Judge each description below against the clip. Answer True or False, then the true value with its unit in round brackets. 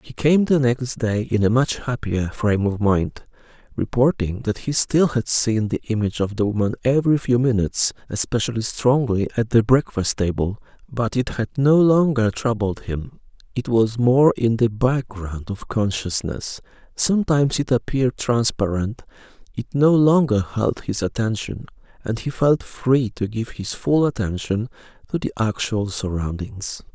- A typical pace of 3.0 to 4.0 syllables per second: False (4.6 syllables/s)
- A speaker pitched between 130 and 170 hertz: False (115 Hz)